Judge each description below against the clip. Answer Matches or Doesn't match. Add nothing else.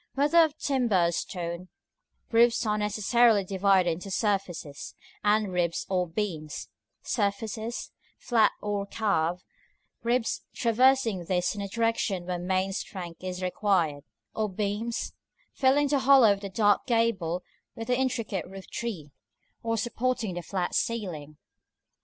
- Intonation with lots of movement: Doesn't match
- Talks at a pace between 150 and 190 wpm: Doesn't match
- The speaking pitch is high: Matches